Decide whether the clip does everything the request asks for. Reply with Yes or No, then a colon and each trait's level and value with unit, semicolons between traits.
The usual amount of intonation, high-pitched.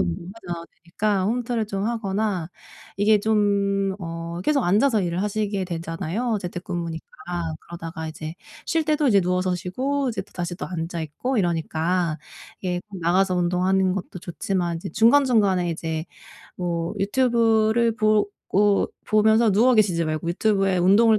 Yes: average, 4.0 semitones; high, 195 Hz